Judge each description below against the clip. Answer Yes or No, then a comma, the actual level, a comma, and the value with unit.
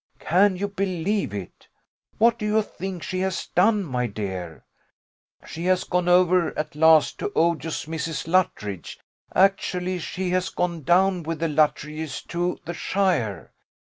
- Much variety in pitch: No, average, 3.2 semitones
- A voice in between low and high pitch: Yes, medium, 175 Hz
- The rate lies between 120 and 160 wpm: Yes, average, 140 wpm